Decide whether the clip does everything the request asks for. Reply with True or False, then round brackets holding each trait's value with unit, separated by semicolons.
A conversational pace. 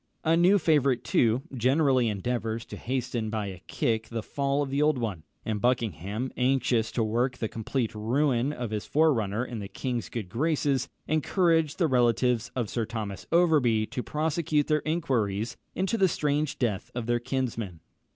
True (170 wpm)